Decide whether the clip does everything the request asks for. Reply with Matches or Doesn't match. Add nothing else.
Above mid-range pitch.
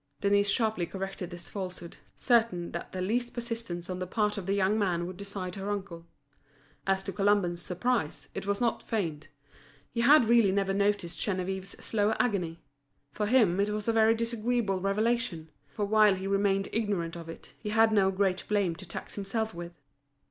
Matches